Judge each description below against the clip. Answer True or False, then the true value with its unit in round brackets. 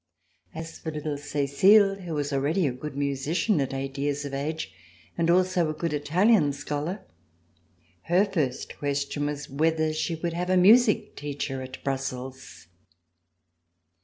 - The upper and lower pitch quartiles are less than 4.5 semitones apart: True (3.6 semitones)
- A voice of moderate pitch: True (150 Hz)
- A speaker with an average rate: True (145 wpm)